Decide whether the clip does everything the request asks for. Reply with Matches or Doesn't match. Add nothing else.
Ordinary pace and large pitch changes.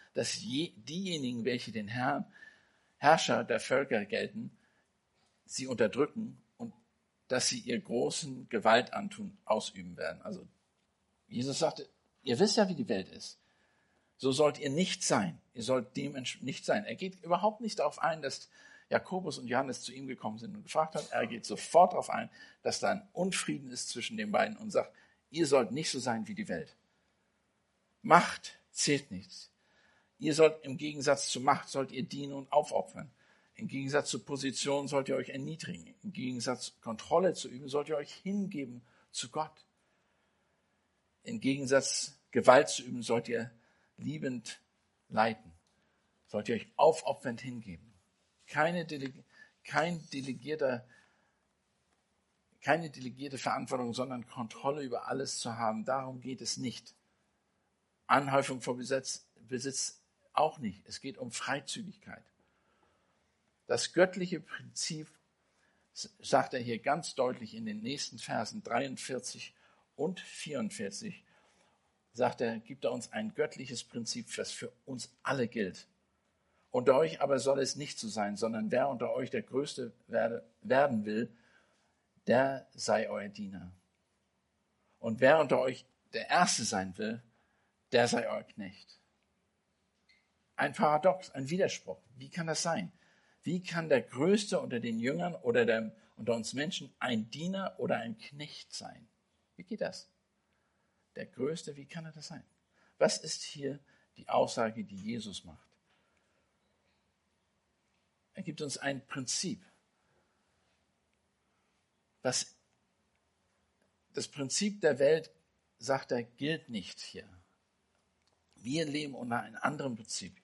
Matches